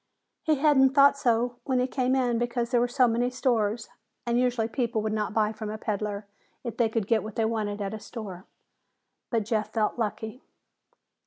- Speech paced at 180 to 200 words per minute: Yes, average, 190 wpm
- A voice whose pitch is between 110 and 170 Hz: No, high, 230 Hz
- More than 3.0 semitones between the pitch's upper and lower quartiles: No, narrow, 2.5 semitones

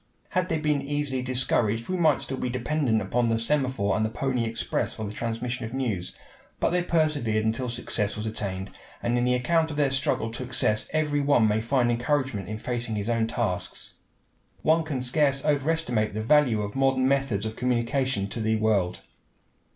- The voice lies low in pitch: Yes, low, 125 Hz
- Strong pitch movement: No, average, 3.9 semitones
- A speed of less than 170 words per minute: No, average, 190 wpm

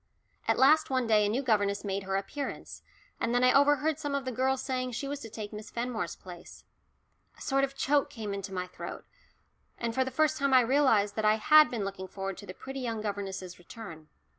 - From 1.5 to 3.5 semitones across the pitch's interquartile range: No, average, 5.1 semitones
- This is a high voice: Yes, high, 230 Hz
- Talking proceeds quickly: Yes, fast, 220 wpm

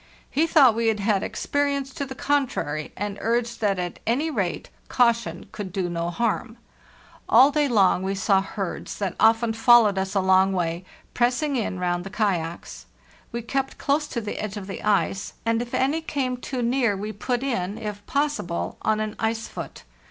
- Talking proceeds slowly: No, average, 180 wpm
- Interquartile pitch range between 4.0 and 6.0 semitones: Yes, average, 4.7 semitones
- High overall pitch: Yes, high, 220 Hz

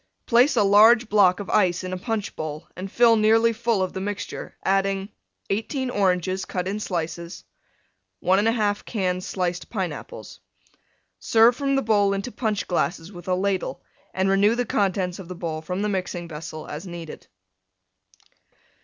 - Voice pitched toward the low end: No, high, 195 Hz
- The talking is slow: No, average, 160 wpm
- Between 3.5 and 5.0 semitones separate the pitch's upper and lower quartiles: No, average, 3.0 semitones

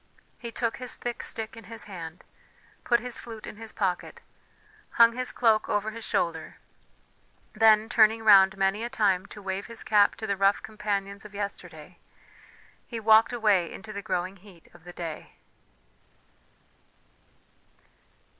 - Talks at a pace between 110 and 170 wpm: Yes, average, 150 wpm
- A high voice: Yes, high, 210 Hz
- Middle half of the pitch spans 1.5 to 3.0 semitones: Yes, average, 2.7 semitones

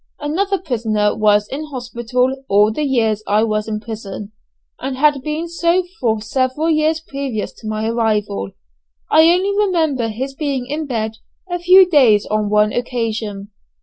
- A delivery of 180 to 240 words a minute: No, average, 155 wpm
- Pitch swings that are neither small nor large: No, wide, 6.0 semitones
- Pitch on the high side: Yes, high, 245 Hz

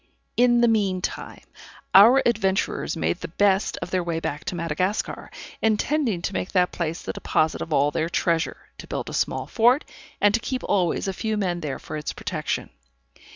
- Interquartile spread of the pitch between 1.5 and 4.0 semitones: No, average, 4.7 semitones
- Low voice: No, high, 190 Hz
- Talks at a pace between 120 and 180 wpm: No, average, 190 wpm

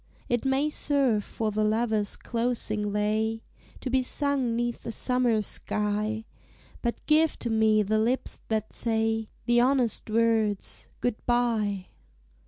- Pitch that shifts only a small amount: Yes, narrow, 2.3 semitones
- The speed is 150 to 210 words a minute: No, slow, 135 wpm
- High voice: Yes, high, 225 Hz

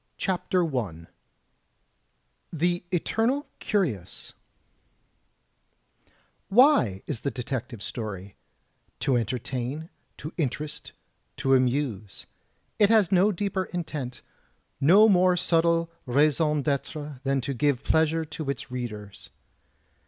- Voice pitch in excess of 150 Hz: No, medium, 145 Hz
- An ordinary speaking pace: No, slow, 100 wpm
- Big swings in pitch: Yes, wide, 5.8 semitones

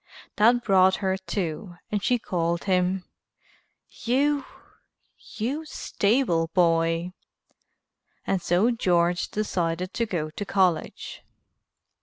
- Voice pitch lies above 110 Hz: Yes, high, 190 Hz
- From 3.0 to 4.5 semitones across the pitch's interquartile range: Yes, average, 3.9 semitones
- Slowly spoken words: Yes, slow, 100 wpm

